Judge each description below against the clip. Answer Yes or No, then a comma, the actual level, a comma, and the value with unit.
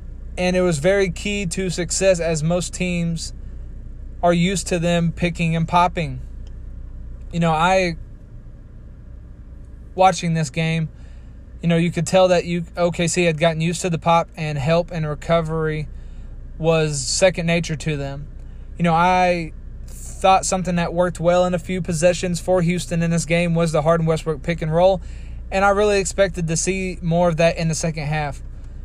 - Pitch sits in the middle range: Yes, medium, 170 Hz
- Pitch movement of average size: No, narrow, 2.1 semitones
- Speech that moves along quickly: No, average, 175 wpm